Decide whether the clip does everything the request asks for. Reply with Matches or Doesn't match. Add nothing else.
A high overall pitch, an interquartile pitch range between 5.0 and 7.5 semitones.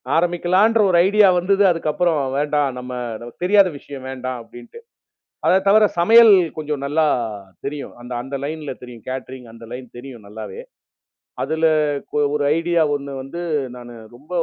Doesn't match